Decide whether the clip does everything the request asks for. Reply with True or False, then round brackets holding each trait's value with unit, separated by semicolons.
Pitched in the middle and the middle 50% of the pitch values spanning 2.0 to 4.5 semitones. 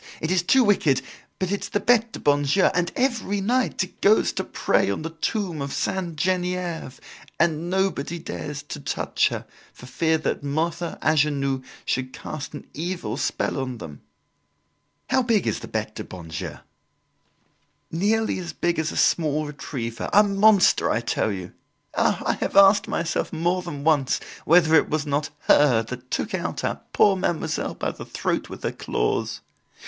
False (165 Hz; 5.0 semitones)